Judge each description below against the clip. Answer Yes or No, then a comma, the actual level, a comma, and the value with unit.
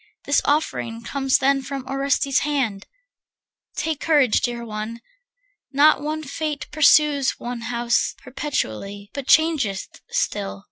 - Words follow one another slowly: Yes, slow, 120 wpm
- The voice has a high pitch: Yes, very high, 270 Hz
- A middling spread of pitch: Yes, average, 4.0 semitones